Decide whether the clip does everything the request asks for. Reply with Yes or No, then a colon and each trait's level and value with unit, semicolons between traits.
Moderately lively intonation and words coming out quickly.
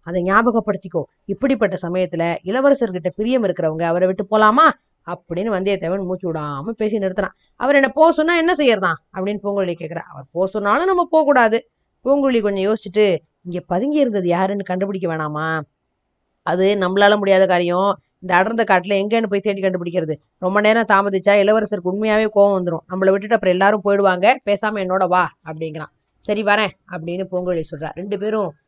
Yes: average, 3.1 semitones; fast, 150 wpm